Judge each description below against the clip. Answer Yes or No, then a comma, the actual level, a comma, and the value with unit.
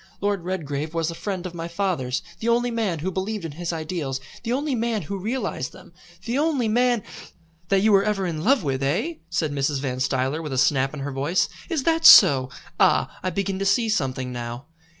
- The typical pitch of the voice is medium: Yes, medium, 175 Hz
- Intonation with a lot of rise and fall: Yes, wide, 7.0 semitones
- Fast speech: Yes, fast, 215 wpm